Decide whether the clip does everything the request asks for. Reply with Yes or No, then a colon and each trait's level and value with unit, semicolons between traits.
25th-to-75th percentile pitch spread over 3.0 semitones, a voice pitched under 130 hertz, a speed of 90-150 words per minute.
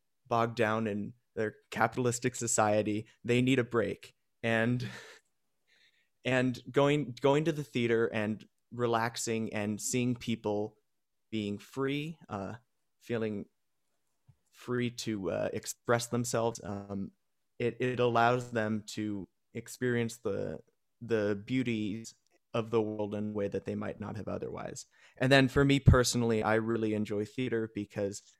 No: narrow, 2.6 semitones; low, 115 Hz; slow, 135 wpm